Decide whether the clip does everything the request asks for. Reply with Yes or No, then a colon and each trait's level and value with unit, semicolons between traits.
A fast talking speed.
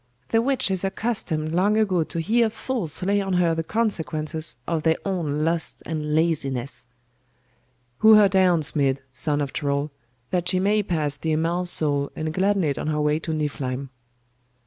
No: average, 170 wpm